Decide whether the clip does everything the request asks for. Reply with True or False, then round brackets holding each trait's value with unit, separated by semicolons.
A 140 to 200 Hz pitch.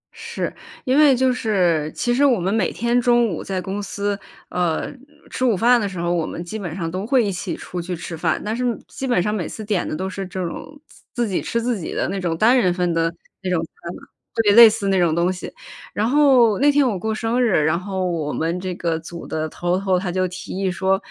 True (190 Hz)